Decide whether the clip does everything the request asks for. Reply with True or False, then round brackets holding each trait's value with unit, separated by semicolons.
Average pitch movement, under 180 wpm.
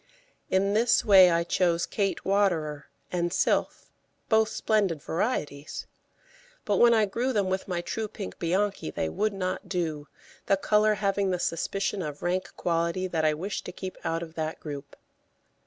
True (3.5 semitones; 165 wpm)